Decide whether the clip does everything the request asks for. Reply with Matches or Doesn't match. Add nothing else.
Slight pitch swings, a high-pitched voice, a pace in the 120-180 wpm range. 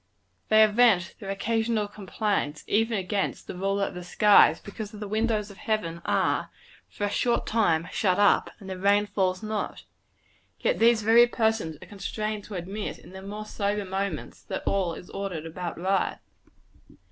Matches